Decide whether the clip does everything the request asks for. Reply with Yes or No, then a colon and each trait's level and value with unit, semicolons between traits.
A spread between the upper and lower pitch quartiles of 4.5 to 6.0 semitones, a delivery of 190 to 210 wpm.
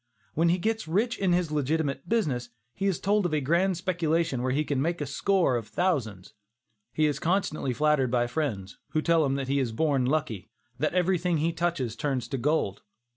Yes: average, 4.9 semitones; fast, 205 wpm